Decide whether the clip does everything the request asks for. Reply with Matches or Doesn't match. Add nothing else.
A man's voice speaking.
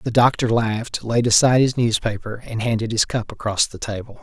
Matches